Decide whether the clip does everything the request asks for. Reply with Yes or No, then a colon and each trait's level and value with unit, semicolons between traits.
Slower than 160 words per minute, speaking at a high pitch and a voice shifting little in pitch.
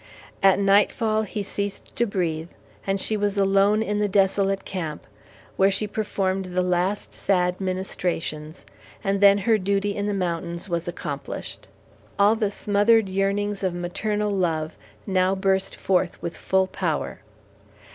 Yes: average, 145 wpm; high, 195 Hz; narrow, 2.0 semitones